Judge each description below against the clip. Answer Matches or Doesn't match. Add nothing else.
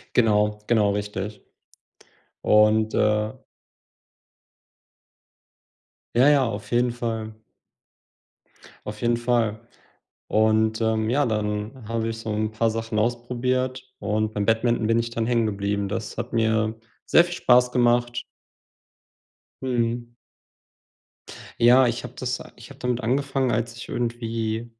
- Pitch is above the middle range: Doesn't match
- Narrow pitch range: Matches